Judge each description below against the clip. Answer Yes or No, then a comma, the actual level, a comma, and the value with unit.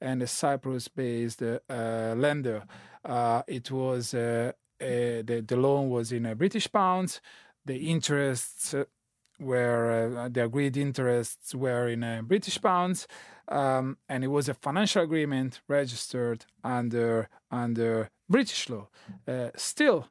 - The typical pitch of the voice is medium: No, low, 125 Hz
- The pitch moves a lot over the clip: No, average, 3.2 semitones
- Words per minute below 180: Yes, slow, 135 wpm